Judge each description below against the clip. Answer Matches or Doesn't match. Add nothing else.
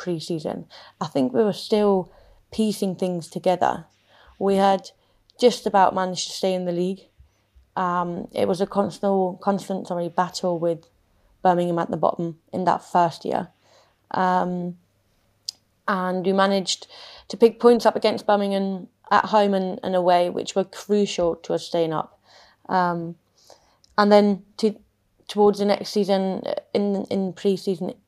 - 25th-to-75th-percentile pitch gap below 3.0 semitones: Matches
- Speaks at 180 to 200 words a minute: Doesn't match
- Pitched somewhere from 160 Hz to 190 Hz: Matches